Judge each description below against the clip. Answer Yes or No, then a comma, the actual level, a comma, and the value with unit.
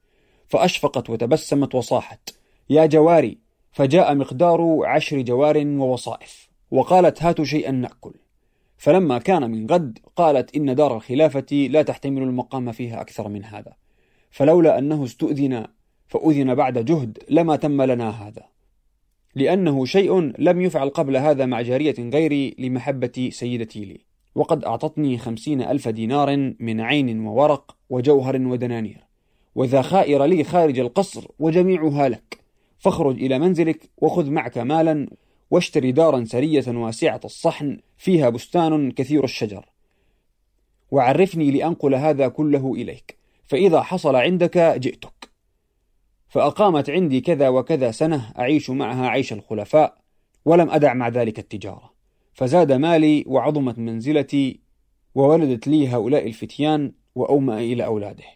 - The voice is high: No, medium, 140 Hz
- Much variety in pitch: No, average, 4.0 semitones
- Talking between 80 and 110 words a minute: No, average, 120 wpm